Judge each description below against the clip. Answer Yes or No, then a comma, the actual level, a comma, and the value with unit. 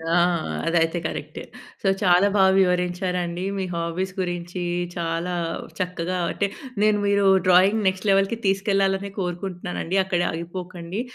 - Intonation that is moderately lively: No, narrow, 1.8 semitones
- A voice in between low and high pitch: Yes, medium, 180 Hz